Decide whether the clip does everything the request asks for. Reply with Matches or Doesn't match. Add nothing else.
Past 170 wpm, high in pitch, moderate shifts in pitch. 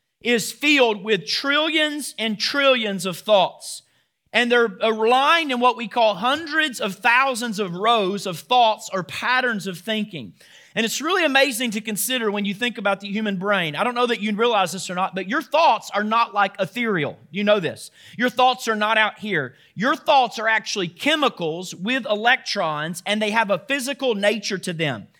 Matches